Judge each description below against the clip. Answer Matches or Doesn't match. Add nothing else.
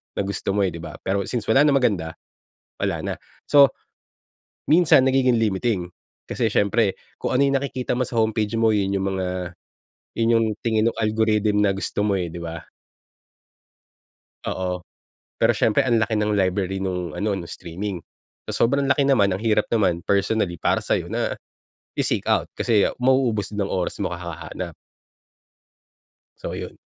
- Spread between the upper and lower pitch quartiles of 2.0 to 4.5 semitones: Matches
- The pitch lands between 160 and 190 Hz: Doesn't match